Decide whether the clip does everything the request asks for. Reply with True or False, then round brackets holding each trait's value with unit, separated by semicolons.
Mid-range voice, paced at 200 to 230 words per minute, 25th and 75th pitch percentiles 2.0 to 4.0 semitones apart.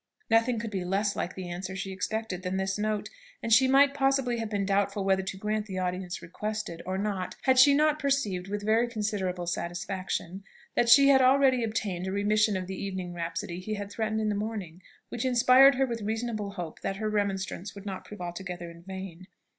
False (205 Hz; 205 wpm; 3.3 semitones)